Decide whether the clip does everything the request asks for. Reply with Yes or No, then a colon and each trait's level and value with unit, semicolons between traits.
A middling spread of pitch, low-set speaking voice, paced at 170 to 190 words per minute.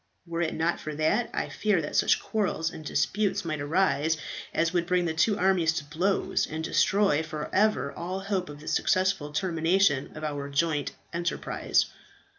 No: average, 3.5 semitones; medium, 165 Hz; average, 175 wpm